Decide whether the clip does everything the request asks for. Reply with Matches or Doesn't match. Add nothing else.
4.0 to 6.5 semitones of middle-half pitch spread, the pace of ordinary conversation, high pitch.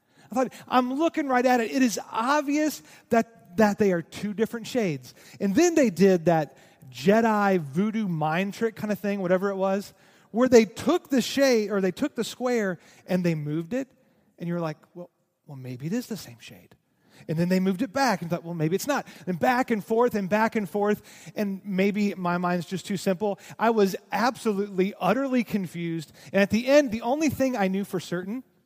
Doesn't match